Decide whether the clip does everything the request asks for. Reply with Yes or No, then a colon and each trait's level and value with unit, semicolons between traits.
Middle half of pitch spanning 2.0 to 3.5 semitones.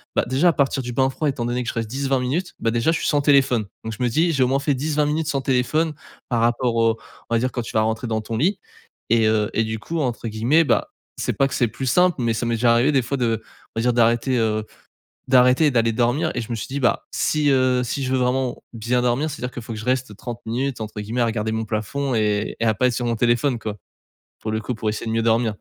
Yes: average, 3.1 semitones